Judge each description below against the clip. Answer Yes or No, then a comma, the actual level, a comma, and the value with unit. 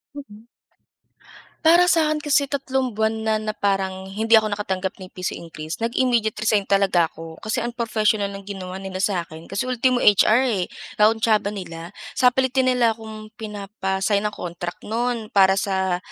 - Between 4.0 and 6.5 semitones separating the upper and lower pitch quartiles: No, average, 3.5 semitones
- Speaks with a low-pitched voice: No, high, 210 Hz